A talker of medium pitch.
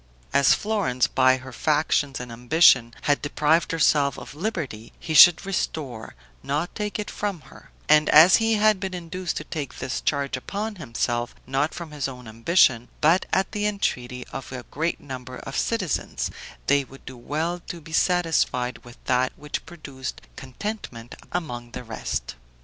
Yes: medium, 145 Hz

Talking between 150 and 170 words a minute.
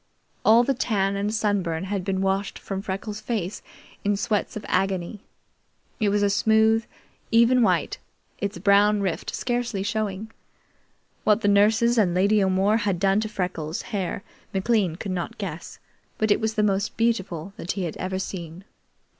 Yes: average, 165 wpm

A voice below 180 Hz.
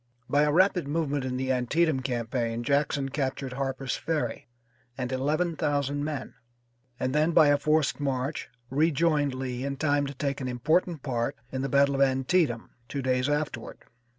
Yes: medium, 140 Hz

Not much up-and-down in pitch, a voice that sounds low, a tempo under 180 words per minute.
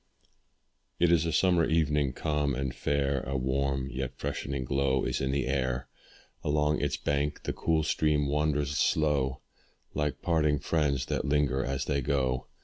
Yes: narrow, 1.9 semitones; very low, 70 Hz; average, 155 wpm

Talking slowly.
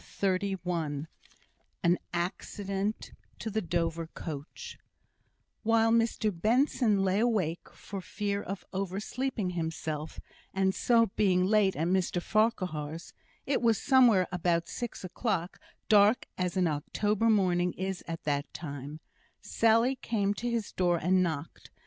Yes: slow, 130 wpm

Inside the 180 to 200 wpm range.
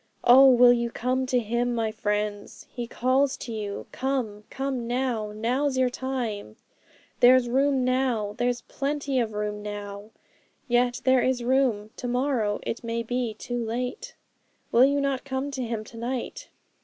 No: average, 160 wpm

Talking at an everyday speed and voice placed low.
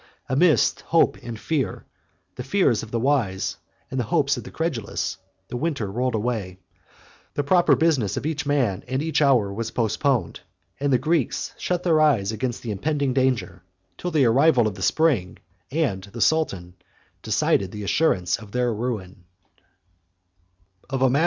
Yes: average, 155 wpm; low, 125 Hz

